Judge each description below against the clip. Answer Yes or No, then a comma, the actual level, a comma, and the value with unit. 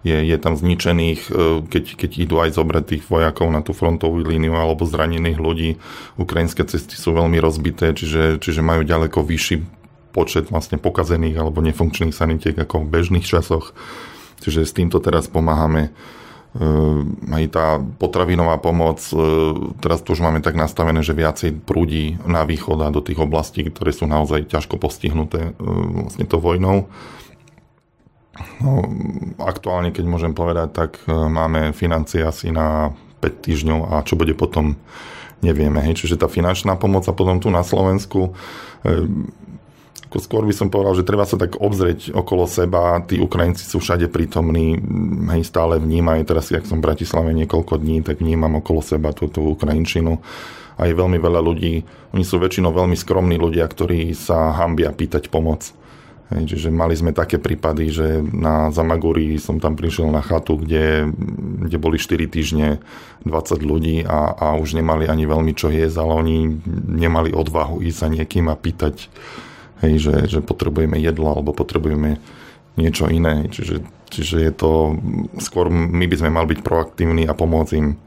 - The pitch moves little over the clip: Yes, narrow, 1.6 semitones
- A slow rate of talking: No, average, 160 wpm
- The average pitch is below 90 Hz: Yes, very low, 80 Hz